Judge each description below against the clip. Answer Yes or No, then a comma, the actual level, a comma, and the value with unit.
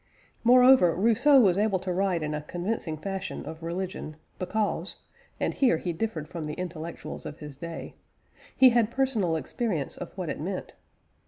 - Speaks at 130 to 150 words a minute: No, average, 165 wpm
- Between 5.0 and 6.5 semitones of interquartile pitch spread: Yes, wide, 5.6 semitones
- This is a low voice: No, medium, 185 Hz